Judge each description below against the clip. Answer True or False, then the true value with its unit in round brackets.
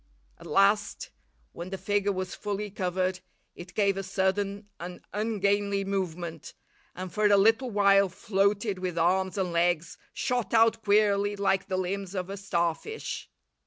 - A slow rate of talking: False (150 wpm)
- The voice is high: True (195 Hz)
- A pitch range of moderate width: False (1.8 semitones)